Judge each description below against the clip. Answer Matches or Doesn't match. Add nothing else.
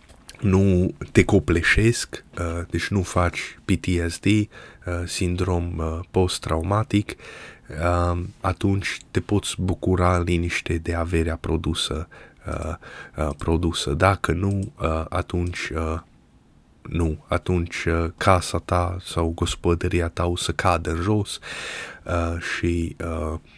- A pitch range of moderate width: Doesn't match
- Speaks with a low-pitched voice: Matches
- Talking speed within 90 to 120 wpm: Matches